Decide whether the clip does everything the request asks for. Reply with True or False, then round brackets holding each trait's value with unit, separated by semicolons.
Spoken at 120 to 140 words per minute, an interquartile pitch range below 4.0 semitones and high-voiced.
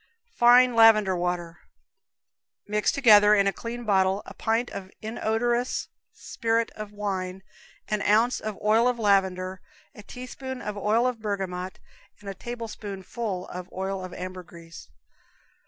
True (135 wpm; 3.4 semitones; 210 Hz)